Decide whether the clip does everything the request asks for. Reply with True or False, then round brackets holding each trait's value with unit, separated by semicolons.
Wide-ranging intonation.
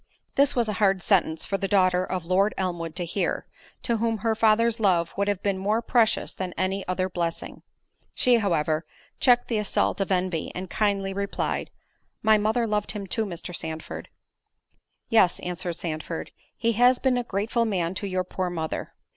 False (3.5 semitones)